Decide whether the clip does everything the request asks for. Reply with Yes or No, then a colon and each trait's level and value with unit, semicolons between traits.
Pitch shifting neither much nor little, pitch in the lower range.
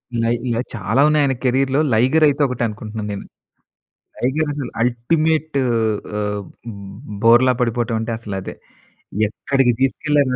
Yes: average, 3.6 semitones; low, 125 Hz